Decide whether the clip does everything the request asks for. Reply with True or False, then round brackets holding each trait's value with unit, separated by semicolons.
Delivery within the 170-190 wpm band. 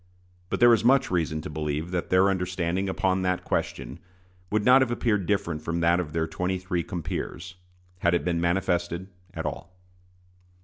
True (175 wpm)